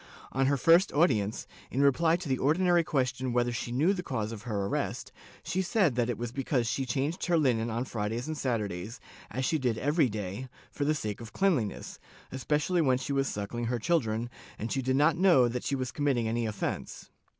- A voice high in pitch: No, low, 130 Hz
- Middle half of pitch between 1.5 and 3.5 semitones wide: No, average, 4.4 semitones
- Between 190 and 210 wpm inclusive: Yes, fast, 205 wpm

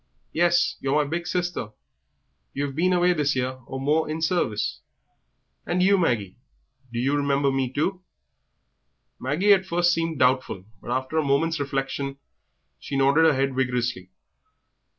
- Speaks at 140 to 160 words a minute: Yes, average, 150 wpm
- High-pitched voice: No, medium, 140 Hz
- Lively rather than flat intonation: No, average, 4.3 semitones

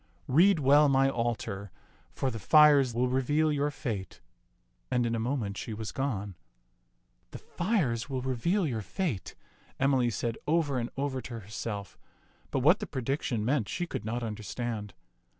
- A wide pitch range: No, average, 4.5 semitones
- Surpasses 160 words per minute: Yes, average, 170 wpm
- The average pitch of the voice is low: Yes, low, 125 Hz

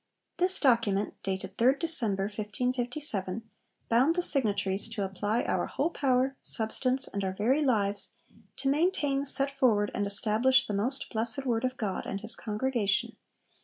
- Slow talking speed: No, average, 150 wpm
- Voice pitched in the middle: No, high, 230 Hz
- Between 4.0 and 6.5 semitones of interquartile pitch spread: Yes, average, 4.7 semitones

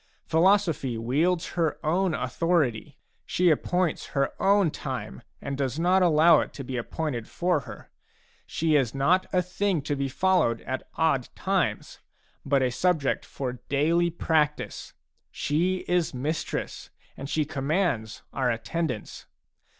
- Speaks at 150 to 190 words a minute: No, slow, 135 wpm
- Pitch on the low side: No, medium, 155 Hz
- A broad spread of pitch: No, average, 4.6 semitones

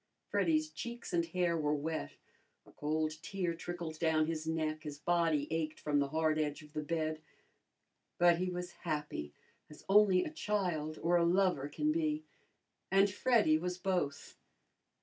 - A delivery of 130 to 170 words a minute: Yes, average, 160 wpm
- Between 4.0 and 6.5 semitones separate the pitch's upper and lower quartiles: No, average, 2.8 semitones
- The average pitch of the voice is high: No, medium, 165 Hz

